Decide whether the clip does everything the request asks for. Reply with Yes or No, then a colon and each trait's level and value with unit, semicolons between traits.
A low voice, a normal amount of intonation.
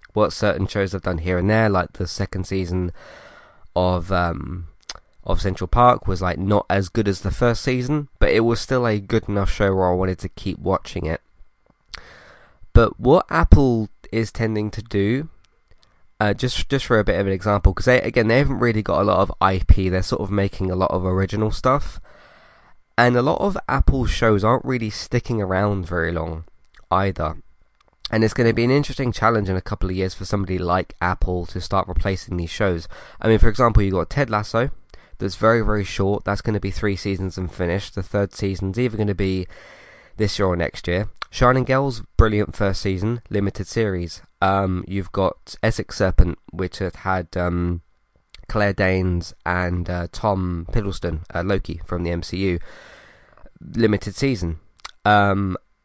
Yes: very low, 95 Hz; average, 3.1 semitones